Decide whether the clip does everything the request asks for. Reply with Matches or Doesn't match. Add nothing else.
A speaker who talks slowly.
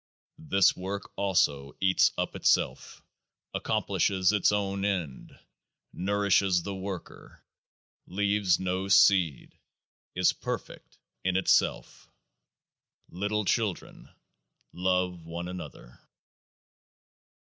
Matches